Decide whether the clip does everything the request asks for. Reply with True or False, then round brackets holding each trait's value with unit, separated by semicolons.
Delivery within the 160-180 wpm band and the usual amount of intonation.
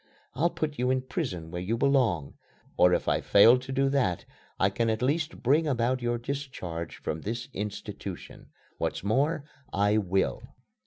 False (165 wpm; 5.8 semitones)